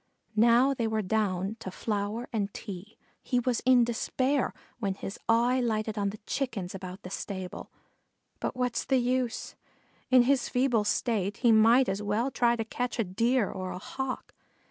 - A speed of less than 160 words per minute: No, average, 170 wpm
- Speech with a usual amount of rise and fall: Yes, average, 3.7 semitones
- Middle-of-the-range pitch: No, high, 225 Hz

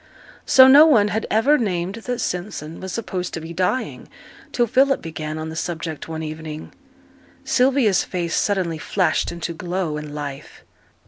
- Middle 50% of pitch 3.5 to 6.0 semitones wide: Yes, wide, 5.6 semitones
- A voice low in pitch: No, medium, 180 Hz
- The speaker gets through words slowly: No, average, 155 wpm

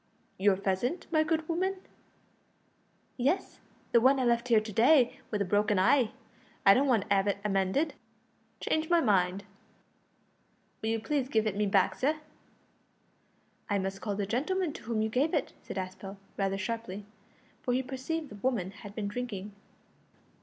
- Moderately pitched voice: No, high, 225 Hz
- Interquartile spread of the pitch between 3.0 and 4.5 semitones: No, average, 5.1 semitones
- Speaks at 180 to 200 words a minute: No, average, 165 wpm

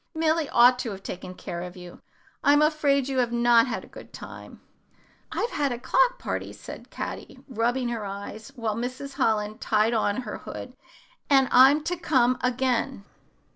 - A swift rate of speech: No, average, 175 wpm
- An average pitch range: Yes, average, 4.1 semitones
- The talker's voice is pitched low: No, high, 245 Hz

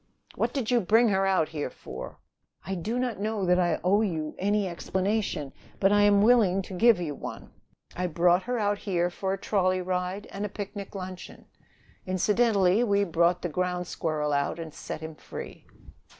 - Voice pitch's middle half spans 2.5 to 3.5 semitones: Yes, average, 2.8 semitones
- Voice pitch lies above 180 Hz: Yes, high, 190 Hz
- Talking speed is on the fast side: No, average, 185 wpm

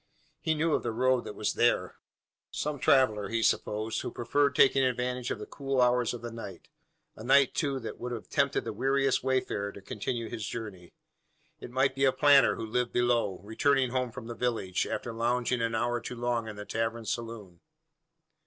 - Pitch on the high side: No, low, 120 Hz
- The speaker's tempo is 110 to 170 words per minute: No, average, 195 wpm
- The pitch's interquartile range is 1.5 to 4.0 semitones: Yes, narrow, 2.5 semitones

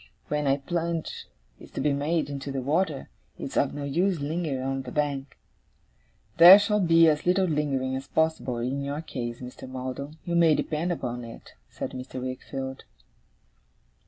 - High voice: No, medium, 145 Hz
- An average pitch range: Yes, average, 3.7 semitones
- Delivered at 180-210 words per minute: No, average, 165 wpm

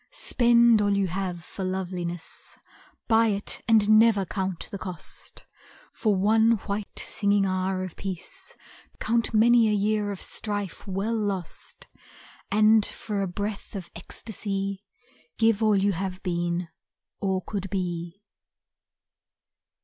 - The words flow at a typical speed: No, slow, 125 wpm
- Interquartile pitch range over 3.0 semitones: No, narrow, 2.5 semitones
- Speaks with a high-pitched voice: Yes, high, 200 Hz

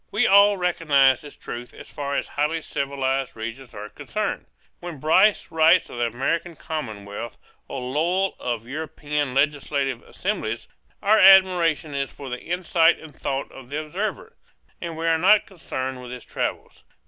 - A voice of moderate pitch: Yes, medium, 150 Hz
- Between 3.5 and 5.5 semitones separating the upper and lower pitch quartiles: Yes, average, 4.9 semitones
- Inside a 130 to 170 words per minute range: Yes, average, 160 wpm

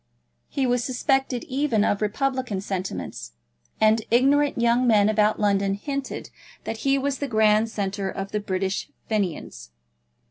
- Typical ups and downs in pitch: Yes, average, 4.5 semitones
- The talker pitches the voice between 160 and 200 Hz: No, high, 220 Hz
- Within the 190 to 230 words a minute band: No, average, 140 wpm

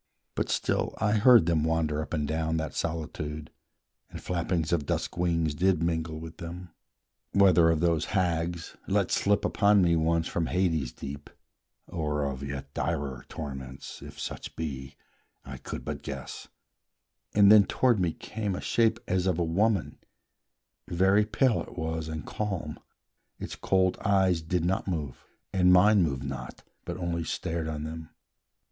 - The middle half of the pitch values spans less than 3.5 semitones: Yes, average, 3.0 semitones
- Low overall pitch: Yes, very low, 85 Hz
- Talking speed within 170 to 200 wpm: No, average, 160 wpm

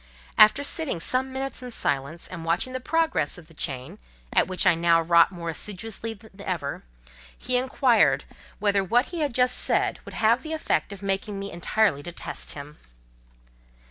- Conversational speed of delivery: Yes, average, 175 wpm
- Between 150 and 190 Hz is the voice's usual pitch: No, high, 200 Hz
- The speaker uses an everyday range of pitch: No, wide, 6.9 semitones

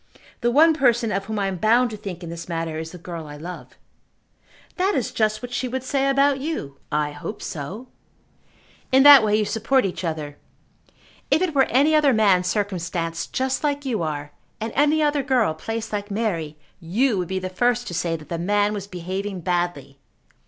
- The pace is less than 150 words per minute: No, average, 200 wpm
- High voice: Yes, high, 205 Hz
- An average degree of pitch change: No, wide, 7.1 semitones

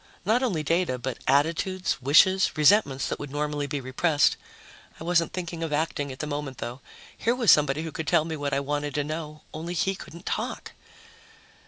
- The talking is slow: No, average, 190 wpm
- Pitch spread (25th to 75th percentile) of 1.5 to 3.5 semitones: Yes, average, 2.9 semitones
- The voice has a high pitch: No, medium, 150 Hz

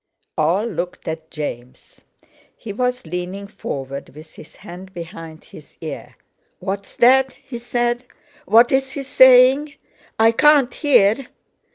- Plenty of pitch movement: Yes, wide, 6.7 semitones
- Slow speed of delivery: Yes, slow, 125 wpm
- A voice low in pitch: No, high, 215 Hz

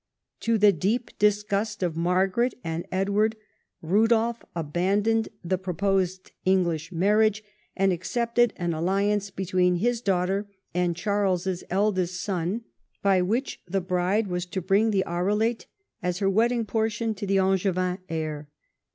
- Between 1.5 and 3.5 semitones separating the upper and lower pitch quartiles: Yes, average, 2.9 semitones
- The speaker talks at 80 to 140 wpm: Yes, slow, 135 wpm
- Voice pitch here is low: No, high, 195 Hz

